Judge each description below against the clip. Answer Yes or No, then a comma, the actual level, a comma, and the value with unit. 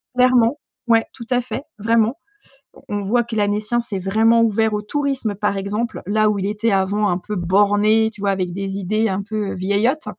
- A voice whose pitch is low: No, high, 210 Hz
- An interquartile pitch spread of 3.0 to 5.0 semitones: No, narrow, 2.4 semitones